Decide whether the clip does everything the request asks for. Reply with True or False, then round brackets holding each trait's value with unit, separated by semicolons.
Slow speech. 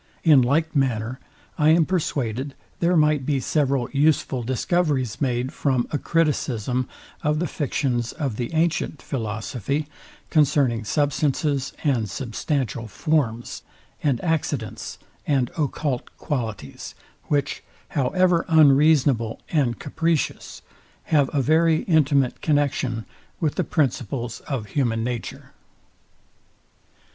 True (110 wpm)